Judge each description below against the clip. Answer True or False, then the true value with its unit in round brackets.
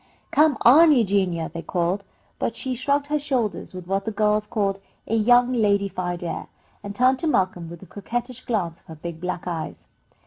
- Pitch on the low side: False (205 Hz)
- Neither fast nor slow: True (185 wpm)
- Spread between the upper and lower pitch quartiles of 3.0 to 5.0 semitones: False (5.5 semitones)